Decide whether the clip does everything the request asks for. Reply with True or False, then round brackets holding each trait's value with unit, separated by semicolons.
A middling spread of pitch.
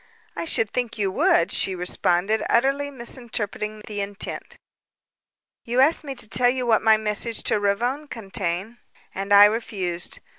True (3.5 semitones)